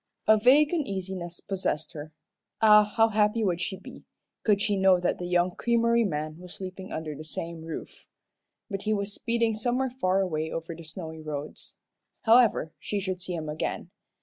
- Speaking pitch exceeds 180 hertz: Yes, high, 190 Hz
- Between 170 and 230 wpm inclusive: Yes, average, 175 wpm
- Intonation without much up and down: No, average, 4.7 semitones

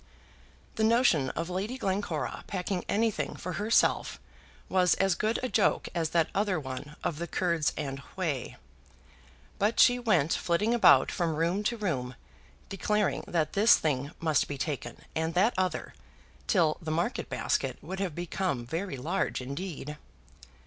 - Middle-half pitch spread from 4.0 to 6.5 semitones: Yes, average, 4.7 semitones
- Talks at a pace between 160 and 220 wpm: No, average, 150 wpm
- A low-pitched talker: No, medium, 175 Hz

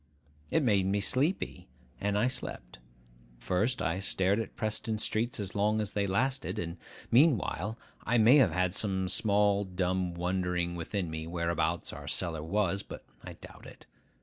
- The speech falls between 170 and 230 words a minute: No, average, 160 wpm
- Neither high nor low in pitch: No, low, 100 Hz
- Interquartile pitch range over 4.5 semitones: No, average, 3.5 semitones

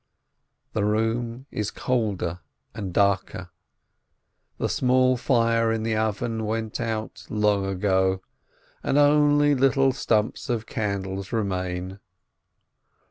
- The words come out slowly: Yes, slow, 105 wpm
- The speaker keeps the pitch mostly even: No, average, 3.4 semitones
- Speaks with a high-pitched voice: No, low, 110 Hz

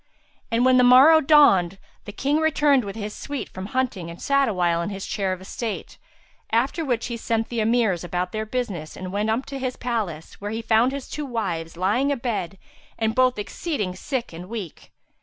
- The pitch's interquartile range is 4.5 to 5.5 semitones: Yes, average, 5.2 semitones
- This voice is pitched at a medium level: No, high, 225 Hz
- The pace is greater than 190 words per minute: Yes, average, 200 wpm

